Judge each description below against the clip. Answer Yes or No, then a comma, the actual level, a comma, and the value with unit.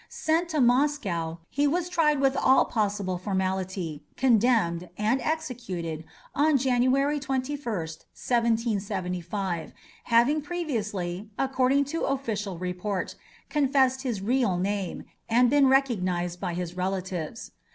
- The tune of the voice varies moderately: No, wide, 6.7 semitones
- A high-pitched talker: Yes, high, 230 Hz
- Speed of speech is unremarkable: No, slow, 110 wpm